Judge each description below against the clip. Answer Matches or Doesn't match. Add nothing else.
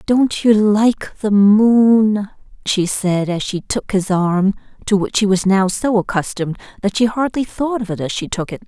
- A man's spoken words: Doesn't match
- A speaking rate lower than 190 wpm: Doesn't match